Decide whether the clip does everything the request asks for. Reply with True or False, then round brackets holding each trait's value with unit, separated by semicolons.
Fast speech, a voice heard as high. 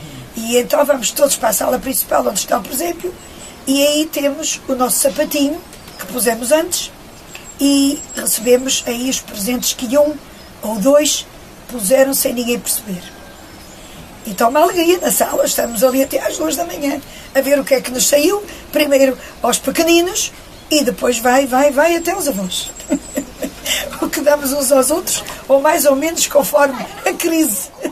False (170 wpm; 280 Hz)